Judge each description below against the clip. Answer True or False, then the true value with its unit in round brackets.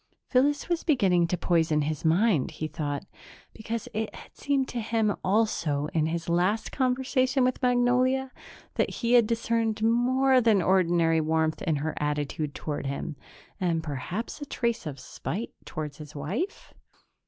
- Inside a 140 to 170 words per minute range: True (155 wpm)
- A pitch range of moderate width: False (7.6 semitones)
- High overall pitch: True (195 Hz)